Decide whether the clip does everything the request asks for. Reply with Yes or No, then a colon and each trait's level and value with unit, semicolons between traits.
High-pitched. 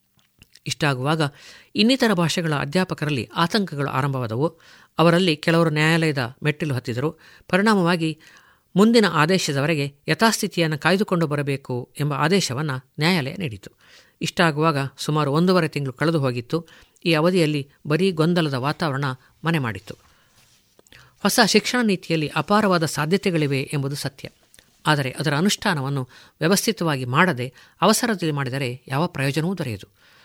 No: medium, 160 Hz